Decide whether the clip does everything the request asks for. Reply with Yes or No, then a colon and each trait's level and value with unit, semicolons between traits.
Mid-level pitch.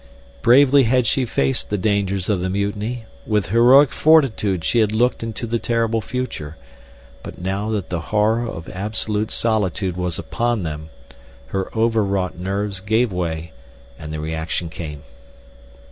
No: low, 105 Hz